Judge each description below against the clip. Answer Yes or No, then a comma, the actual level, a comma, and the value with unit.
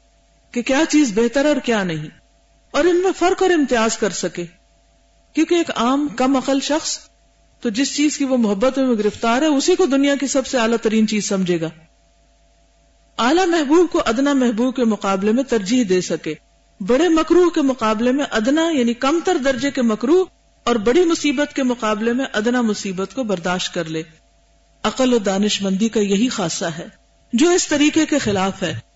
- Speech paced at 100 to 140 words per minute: No, average, 185 wpm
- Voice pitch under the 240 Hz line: No, high, 245 Hz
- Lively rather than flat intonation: Yes, wide, 6.0 semitones